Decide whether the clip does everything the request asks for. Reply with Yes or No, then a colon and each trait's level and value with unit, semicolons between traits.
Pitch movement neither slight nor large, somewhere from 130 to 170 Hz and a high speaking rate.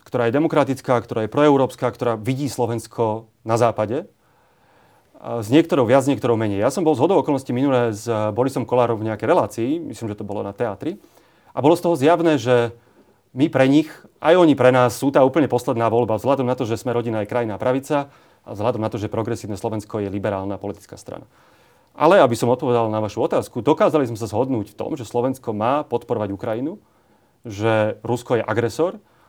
No: average, 3.1 semitones; low, 120 Hz; fast, 200 wpm